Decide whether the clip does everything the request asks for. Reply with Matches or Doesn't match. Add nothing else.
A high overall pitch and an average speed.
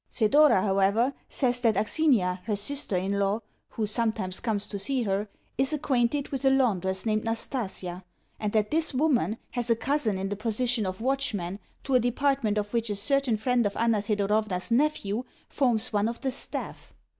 Matches